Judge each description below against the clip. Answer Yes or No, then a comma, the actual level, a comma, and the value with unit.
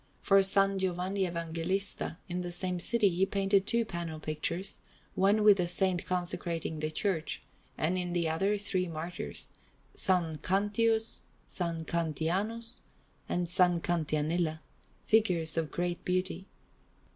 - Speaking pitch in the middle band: Yes, medium, 180 Hz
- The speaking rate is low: Yes, slow, 130 wpm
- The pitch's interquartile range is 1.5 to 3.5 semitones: Yes, narrow, 2.6 semitones